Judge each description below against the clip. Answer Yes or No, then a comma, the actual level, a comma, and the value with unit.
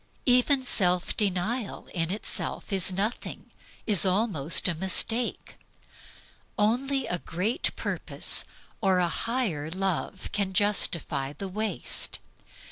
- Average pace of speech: No, slow, 110 wpm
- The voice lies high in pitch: Yes, high, 195 Hz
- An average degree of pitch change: Yes, average, 4.0 semitones